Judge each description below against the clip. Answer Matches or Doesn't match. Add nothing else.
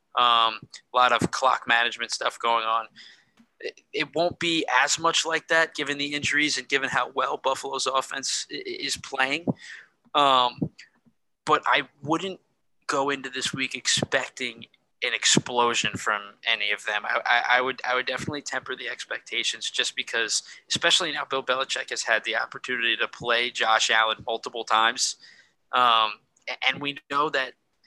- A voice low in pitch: Matches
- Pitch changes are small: Doesn't match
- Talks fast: Doesn't match